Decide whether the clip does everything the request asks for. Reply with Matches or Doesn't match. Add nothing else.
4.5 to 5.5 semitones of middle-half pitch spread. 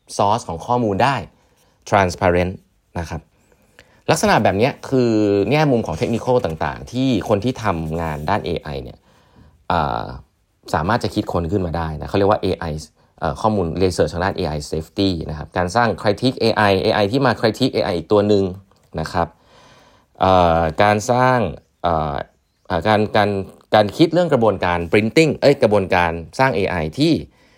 Matches